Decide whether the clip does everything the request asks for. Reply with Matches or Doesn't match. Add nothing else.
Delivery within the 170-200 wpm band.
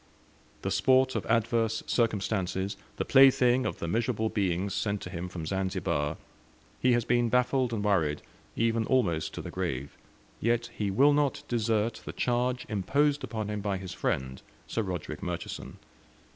Doesn't match